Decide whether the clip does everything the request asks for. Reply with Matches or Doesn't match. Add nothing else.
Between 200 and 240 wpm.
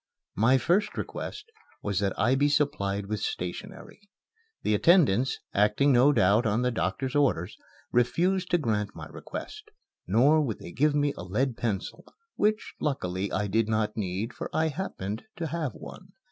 Doesn't match